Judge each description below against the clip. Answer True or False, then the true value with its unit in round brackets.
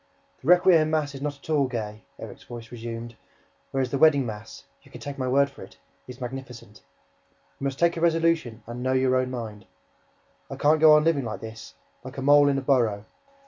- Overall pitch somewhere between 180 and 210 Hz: False (130 Hz)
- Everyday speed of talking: False (210 wpm)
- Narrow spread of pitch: False (3.7 semitones)